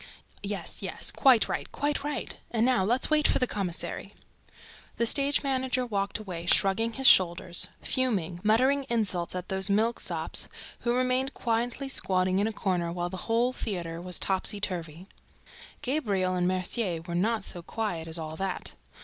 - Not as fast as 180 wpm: Yes, average, 160 wpm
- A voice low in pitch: No, high, 205 Hz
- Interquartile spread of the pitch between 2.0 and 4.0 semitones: No, average, 5.3 semitones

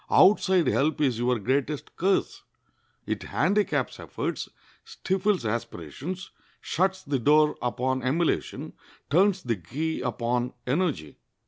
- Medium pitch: Yes, medium, 145 Hz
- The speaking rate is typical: No, slow, 110 wpm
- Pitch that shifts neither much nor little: No, wide, 7.1 semitones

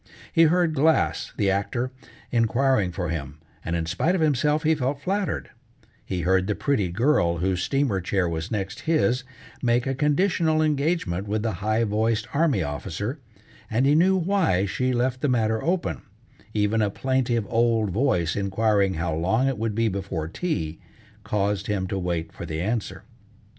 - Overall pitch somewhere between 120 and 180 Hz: No, low, 110 Hz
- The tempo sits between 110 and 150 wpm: No, average, 170 wpm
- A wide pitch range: Yes, wide, 6.6 semitones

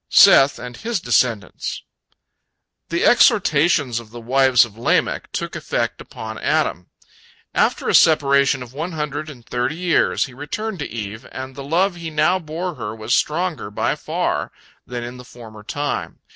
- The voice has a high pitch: No, low, 135 Hz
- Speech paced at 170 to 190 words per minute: No, average, 160 wpm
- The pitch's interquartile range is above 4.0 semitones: Yes, average, 5.1 semitones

